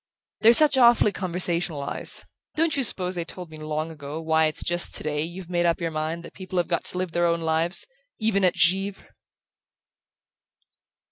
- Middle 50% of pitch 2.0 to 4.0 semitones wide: Yes, average, 2.9 semitones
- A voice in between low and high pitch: Yes, medium, 175 Hz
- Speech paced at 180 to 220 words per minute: Yes, average, 185 wpm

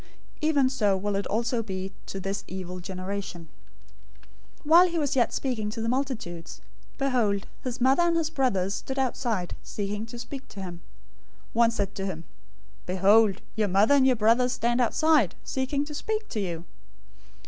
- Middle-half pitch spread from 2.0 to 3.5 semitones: No, wide, 5.4 semitones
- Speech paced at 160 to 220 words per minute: Yes, average, 170 wpm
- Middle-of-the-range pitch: No, high, 225 Hz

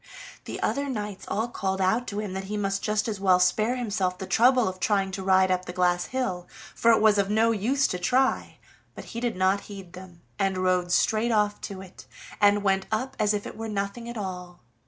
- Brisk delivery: Yes, fast, 225 wpm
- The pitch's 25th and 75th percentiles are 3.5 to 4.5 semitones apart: No, average, 2.8 semitones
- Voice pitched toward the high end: Yes, high, 200 Hz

